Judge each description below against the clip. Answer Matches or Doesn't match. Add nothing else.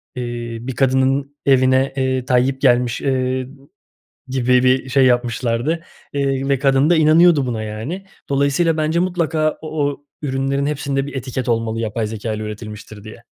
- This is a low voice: Matches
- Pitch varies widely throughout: Doesn't match